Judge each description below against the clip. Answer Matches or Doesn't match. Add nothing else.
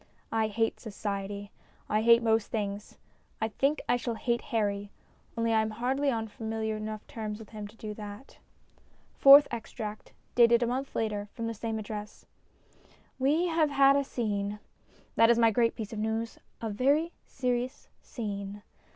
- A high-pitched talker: Matches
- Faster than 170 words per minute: Doesn't match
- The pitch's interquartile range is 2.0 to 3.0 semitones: Matches